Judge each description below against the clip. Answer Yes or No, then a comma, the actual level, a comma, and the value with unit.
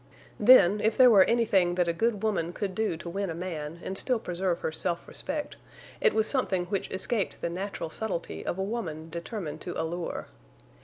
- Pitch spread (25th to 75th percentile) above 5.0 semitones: No, average, 4.3 semitones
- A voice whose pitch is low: No, high, 190 Hz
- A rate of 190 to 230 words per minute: Yes, average, 195 wpm